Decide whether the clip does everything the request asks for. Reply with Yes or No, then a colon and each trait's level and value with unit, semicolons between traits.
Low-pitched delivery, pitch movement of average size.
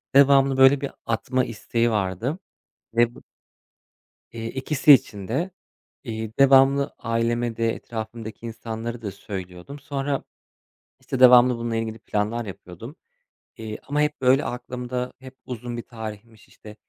Yes: low, 120 Hz; average, 3.1 semitones